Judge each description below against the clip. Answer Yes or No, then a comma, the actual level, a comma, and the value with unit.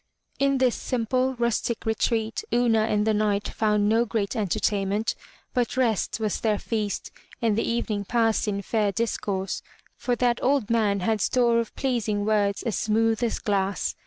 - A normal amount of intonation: No, narrow, 2.2 semitones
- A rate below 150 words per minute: No, average, 160 wpm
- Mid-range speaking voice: No, high, 220 Hz